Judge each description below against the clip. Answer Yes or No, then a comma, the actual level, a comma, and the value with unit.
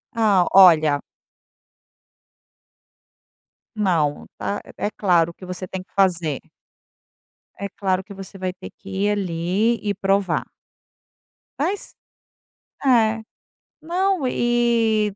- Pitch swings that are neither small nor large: Yes, average, 3.5 semitones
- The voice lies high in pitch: Yes, high, 195 Hz